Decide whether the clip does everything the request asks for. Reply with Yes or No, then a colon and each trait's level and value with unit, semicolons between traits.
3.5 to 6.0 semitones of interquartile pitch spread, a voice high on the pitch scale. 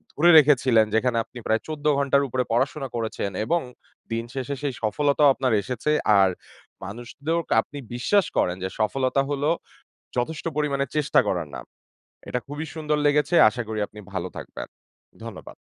No: average, 4.3 semitones; low, 135 Hz